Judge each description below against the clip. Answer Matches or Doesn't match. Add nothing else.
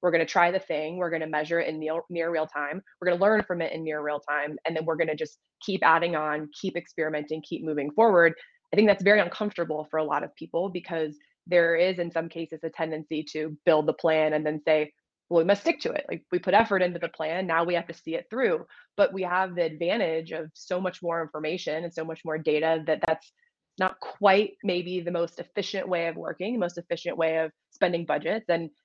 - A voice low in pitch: Doesn't match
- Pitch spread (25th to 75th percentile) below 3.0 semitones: Matches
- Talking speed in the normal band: Doesn't match